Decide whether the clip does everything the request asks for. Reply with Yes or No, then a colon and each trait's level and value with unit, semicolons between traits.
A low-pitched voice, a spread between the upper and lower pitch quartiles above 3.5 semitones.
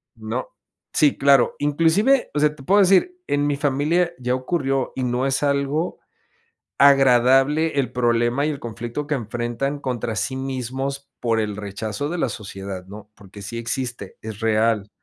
Yes: low, 130 Hz; average, 3.9 semitones